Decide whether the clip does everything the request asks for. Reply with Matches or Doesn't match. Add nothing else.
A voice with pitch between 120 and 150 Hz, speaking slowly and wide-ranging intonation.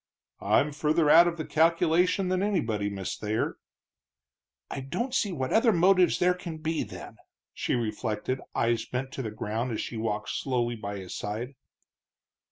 Doesn't match